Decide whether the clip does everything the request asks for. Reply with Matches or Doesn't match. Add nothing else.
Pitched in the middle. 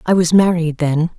Matches